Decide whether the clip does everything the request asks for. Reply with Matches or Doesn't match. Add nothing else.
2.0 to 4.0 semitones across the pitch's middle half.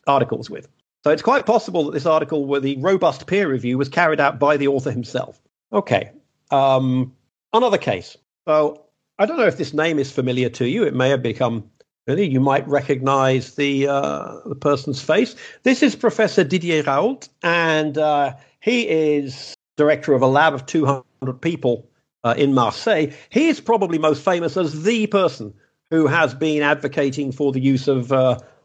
Matches